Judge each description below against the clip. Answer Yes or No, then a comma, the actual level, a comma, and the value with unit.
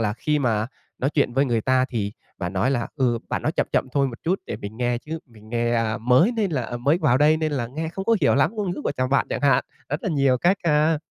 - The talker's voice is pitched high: No, low, 130 Hz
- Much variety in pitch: No, average, 4.6 semitones